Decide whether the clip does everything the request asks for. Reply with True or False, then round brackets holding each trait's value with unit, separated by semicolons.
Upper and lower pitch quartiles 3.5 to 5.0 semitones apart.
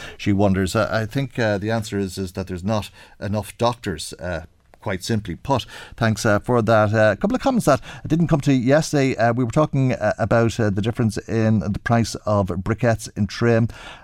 False (2.9 semitones)